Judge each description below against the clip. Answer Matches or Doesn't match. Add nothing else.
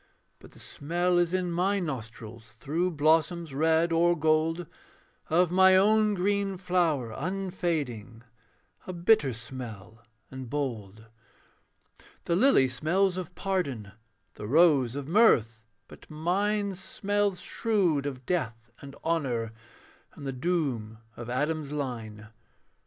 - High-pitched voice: Doesn't match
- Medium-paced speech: Doesn't match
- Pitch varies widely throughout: Matches